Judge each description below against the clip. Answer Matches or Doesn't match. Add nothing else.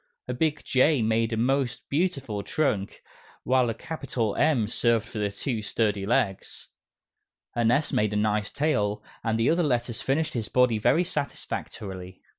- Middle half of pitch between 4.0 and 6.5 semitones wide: Matches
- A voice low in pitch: Matches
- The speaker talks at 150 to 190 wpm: Matches